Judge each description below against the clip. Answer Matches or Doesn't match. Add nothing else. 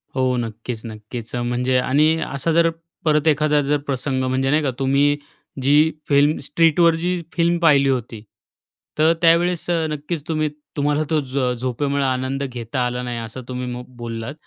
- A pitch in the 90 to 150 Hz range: Matches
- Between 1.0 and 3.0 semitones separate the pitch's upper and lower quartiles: Doesn't match